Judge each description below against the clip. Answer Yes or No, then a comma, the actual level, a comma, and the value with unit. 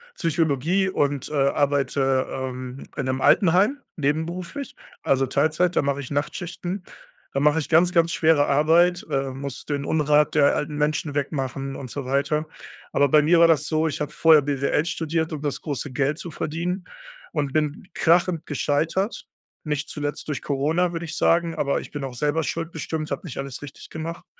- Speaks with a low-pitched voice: No, medium, 150 Hz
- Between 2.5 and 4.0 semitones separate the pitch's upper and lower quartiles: Yes, average, 2.9 semitones